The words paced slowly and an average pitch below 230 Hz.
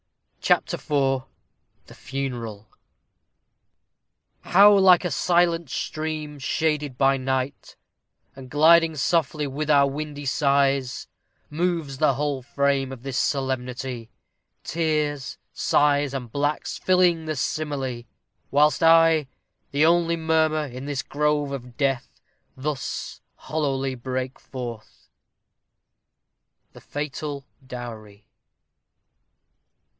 Yes: slow, 100 wpm; medium, 140 Hz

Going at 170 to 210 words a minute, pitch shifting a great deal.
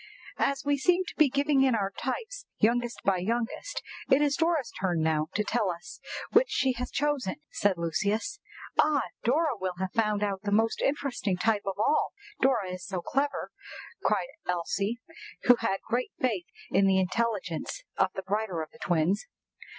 Yes: average, 175 wpm; wide, 6.4 semitones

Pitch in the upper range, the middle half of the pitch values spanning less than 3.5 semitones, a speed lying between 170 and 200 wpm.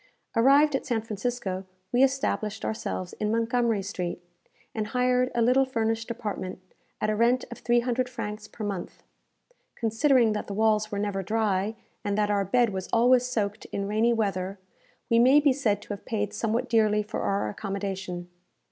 Yes: high, 220 Hz; average, 3.0 semitones; average, 175 wpm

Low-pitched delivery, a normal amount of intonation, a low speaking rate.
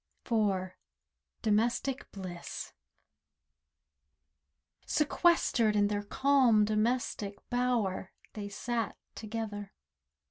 No: high, 215 Hz; average, 3.0 semitones; slow, 70 wpm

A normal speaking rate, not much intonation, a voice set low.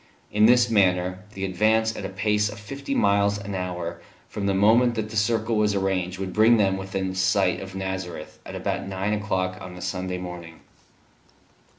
Yes: average, 185 wpm; narrow, 2.3 semitones; very low, 95 Hz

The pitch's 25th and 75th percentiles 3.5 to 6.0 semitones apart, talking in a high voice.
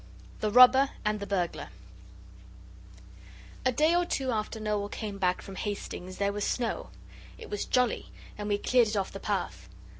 Yes: average, 3.8 semitones; high, 210 Hz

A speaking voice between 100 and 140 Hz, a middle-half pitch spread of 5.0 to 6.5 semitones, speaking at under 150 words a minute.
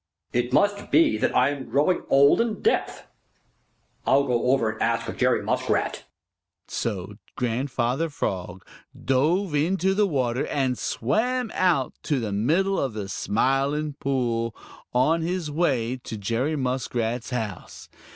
Yes: low, 135 Hz; wide, 5.6 semitones; slow, 135 wpm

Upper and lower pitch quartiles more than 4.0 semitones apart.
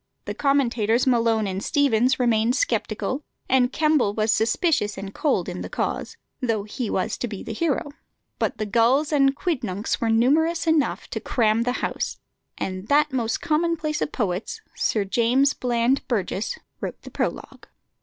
Yes: average, 4.7 semitones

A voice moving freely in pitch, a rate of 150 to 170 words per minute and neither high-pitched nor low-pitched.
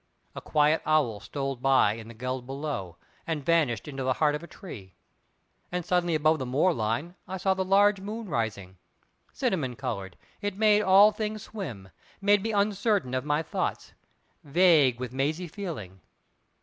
Yes: wide, 7.1 semitones; average, 165 wpm; medium, 150 Hz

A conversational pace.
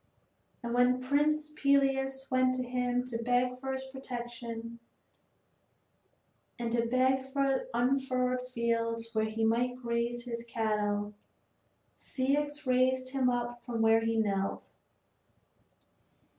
No: slow, 115 wpm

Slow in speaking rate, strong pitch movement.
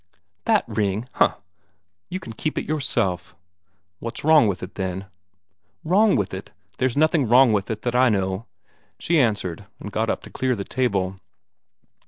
No: average, 165 wpm; wide, 5.7 semitones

